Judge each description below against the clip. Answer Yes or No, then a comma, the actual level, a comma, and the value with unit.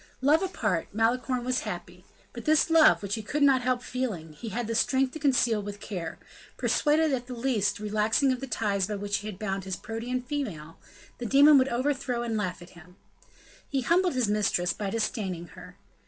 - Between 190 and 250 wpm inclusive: Yes, average, 200 wpm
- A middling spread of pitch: Yes, average, 4.6 semitones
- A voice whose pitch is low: No, high, 230 Hz